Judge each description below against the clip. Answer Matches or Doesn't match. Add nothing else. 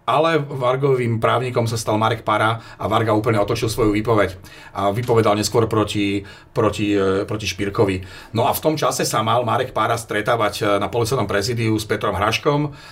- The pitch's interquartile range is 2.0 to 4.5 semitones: Matches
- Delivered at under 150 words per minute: Doesn't match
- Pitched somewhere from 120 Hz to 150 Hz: Doesn't match